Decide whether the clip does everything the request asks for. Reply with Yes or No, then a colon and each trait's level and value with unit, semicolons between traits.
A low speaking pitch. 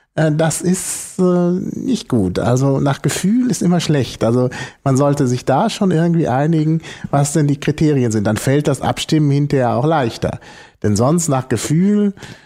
No: medium, 145 Hz